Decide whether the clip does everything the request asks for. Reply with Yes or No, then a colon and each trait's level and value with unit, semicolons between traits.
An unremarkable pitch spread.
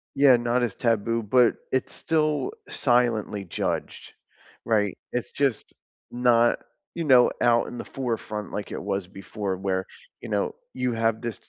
Yes: average, 3.0 semitones